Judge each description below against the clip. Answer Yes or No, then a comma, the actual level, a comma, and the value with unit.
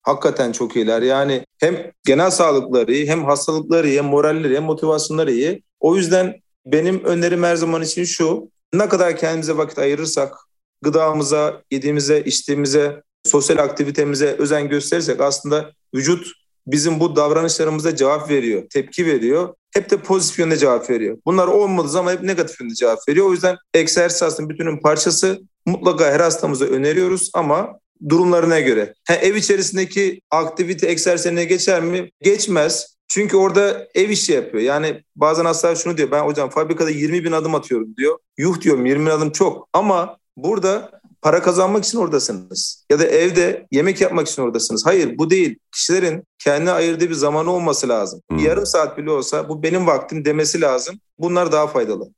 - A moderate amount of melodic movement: Yes, average, 3.4 semitones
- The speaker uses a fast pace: Yes, fast, 160 wpm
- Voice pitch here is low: No, medium, 165 Hz